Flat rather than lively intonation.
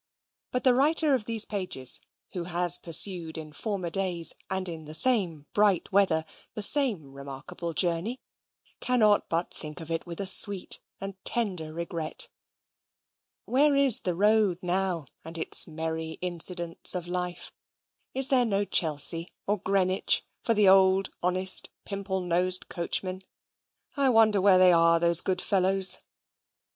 No: average, 3.3 semitones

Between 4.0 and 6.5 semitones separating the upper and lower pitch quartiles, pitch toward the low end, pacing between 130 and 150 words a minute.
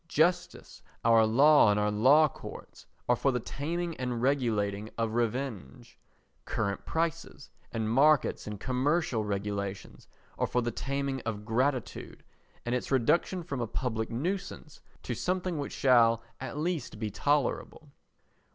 Yes: average, 5.0 semitones; low, 125 Hz; average, 140 wpm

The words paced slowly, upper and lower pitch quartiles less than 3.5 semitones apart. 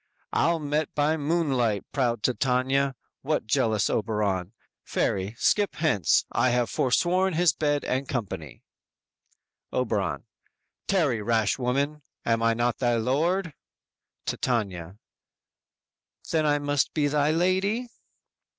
No: slow, 115 wpm; average, 5.2 semitones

